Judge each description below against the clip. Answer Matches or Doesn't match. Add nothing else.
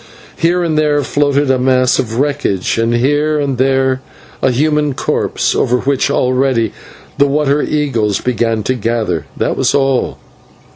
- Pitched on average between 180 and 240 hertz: Doesn't match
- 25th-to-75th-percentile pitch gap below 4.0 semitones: Matches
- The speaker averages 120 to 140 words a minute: Doesn't match